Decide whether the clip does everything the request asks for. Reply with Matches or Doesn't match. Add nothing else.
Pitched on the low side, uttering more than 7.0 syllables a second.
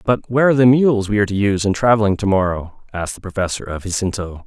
Matches